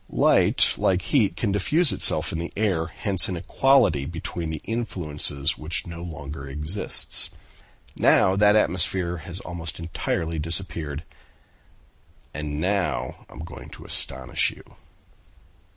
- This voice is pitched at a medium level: No, very low, 85 Hz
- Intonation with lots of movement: No, average, 3.9 semitones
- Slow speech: Yes, slow, 130 wpm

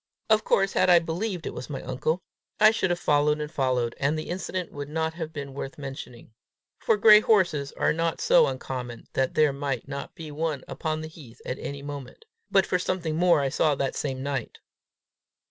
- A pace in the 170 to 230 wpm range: Yes, average, 200 wpm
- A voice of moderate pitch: Yes, medium, 150 Hz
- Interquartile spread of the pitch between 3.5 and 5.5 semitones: Yes, average, 4.2 semitones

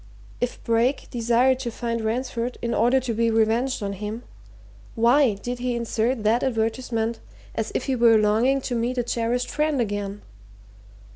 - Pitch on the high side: Yes, high, 235 Hz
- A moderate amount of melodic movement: No, narrow, 1.9 semitones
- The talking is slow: No, average, 160 wpm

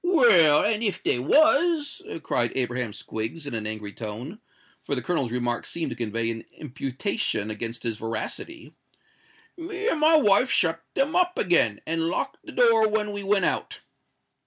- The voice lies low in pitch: No, medium, 170 Hz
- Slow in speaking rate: No, average, 155 wpm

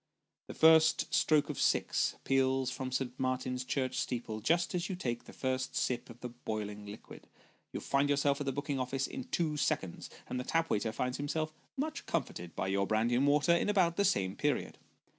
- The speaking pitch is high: No, low, 130 Hz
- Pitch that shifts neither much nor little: Yes, average, 4.3 semitones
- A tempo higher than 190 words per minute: Yes, average, 200 wpm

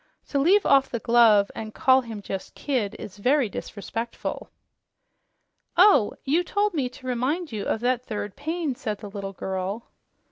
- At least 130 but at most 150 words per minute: No, average, 165 wpm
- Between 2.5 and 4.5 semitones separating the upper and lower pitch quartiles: No, average, 5.3 semitones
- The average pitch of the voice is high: Yes, high, 240 Hz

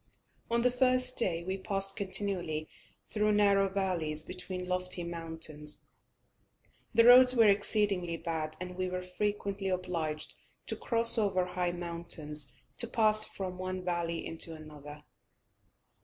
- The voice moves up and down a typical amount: Yes, average, 3.6 semitones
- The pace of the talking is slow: Yes, slow, 130 wpm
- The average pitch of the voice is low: No, medium, 185 Hz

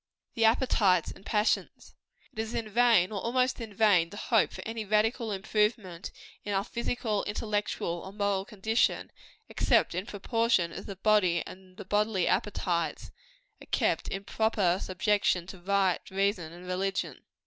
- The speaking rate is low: No, average, 155 wpm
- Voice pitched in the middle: No, high, 205 Hz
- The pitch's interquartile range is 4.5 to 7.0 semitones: No, average, 2.9 semitones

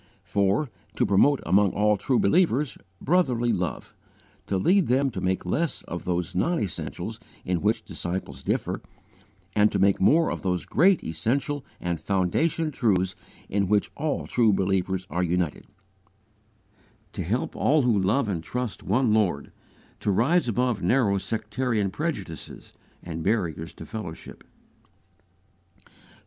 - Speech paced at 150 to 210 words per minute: No, slow, 135 wpm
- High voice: No, low, 105 Hz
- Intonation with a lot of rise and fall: Yes, wide, 5.9 semitones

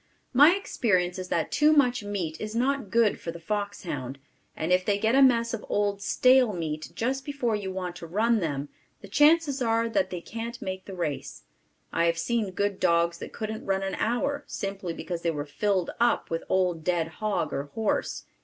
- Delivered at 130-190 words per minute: No, average, 200 wpm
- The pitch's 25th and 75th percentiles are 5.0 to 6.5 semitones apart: Yes, average, 5.3 semitones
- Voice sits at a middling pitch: No, high, 200 Hz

